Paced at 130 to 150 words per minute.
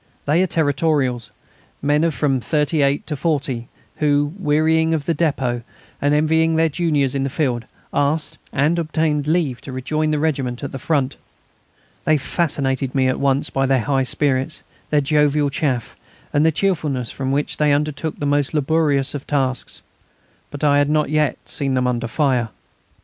No: average, 170 wpm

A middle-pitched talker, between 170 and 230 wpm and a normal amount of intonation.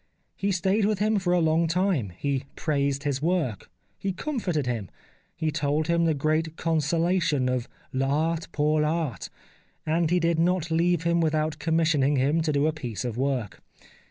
Yes: medium, 155 Hz; average, 180 wpm; average, 3.1 semitones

